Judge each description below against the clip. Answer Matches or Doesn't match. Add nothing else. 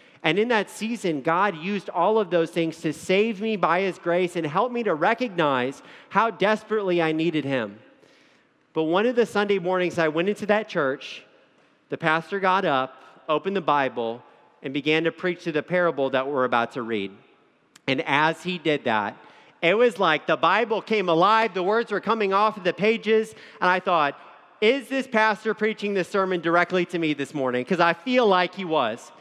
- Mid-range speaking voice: Matches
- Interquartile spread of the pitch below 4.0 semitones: Doesn't match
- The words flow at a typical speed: Matches